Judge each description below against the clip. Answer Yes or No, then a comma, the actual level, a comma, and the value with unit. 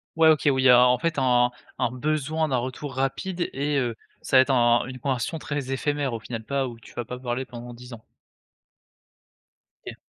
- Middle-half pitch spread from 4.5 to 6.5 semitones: No, average, 2.9 semitones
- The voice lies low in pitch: Yes, low, 130 Hz